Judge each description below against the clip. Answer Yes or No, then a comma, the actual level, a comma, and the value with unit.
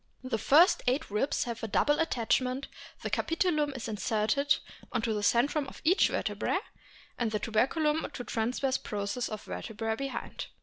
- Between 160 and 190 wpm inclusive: No, average, 150 wpm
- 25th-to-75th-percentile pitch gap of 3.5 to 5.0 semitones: Yes, average, 4.6 semitones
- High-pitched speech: Yes, very high, 250 Hz